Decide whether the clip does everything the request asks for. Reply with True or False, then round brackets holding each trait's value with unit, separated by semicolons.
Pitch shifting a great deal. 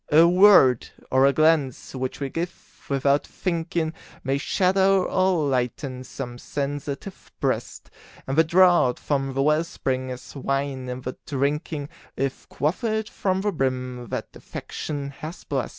False (4.2 semitones)